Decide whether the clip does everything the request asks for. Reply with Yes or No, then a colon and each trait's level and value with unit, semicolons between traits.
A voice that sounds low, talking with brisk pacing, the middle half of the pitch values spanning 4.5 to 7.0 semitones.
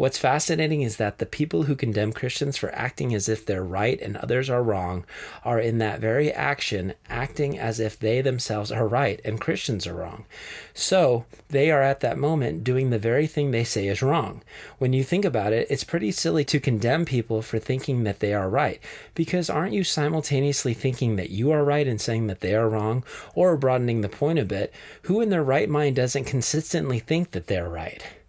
Yes: low, 130 Hz; fast, 210 wpm; average, 4.9 semitones